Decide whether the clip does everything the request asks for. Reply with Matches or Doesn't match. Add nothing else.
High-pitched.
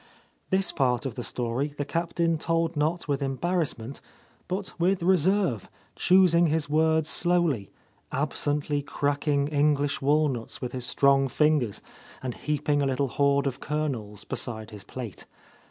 Doesn't match